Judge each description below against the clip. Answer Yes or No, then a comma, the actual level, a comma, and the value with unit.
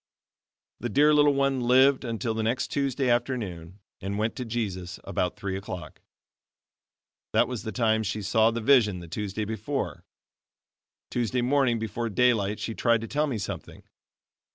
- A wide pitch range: No, average, 3.4 semitones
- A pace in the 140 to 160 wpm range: Yes, average, 155 wpm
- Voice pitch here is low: Yes, low, 115 Hz